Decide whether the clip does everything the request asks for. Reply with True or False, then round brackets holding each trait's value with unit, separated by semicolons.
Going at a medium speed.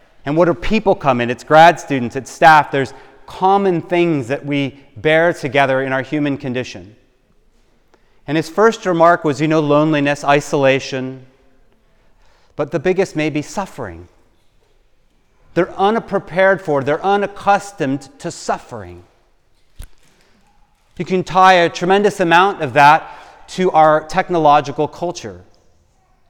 False (130 wpm)